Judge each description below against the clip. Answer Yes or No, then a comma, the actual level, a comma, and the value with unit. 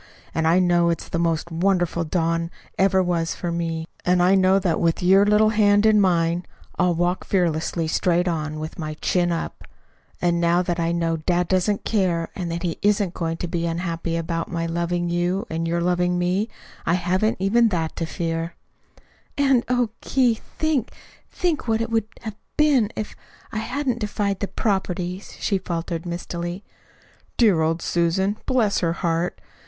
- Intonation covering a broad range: No, average, 3.1 semitones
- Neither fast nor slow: Yes, average, 175 wpm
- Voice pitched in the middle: Yes, medium, 175 Hz